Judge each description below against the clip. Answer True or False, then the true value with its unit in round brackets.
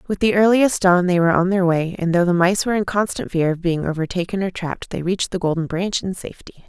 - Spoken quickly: True (260 wpm)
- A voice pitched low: False (180 Hz)